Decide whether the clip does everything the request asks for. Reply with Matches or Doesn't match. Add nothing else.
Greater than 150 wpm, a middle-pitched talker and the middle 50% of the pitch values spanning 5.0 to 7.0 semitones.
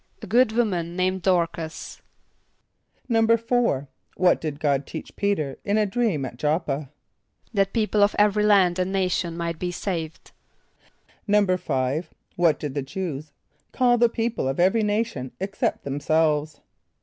Doesn't match